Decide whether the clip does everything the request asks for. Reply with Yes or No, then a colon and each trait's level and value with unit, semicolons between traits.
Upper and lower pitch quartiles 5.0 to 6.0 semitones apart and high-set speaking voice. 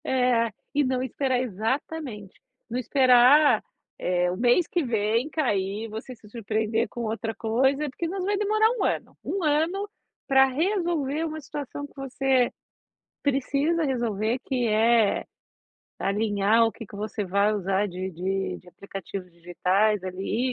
Yes: average, 5.3 semitones; high, 240 Hz